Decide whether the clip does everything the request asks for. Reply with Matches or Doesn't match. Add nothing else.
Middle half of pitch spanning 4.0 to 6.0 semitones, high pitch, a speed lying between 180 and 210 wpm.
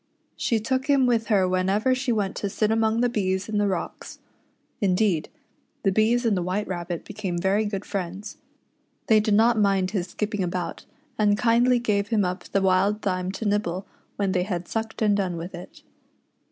Doesn't match